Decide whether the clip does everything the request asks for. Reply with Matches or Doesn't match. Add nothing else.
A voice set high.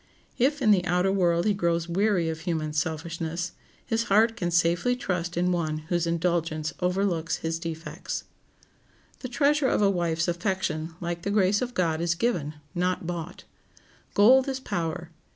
Doesn't match